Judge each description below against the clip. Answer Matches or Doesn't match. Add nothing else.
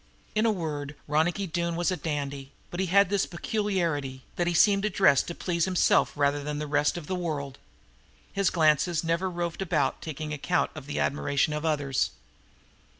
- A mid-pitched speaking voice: Matches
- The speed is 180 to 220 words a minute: Matches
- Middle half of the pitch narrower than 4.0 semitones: Matches